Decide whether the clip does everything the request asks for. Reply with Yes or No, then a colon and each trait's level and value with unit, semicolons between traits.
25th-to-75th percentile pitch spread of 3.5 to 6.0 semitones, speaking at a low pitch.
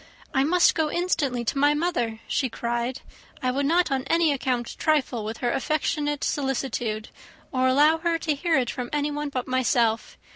No: average, 3.8 semitones; very high, 275 Hz